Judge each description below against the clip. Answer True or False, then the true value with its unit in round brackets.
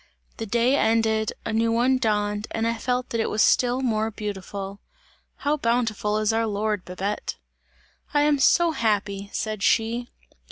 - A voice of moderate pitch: False (225 Hz)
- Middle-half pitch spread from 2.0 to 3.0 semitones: True (2.5 semitones)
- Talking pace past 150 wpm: True (160 wpm)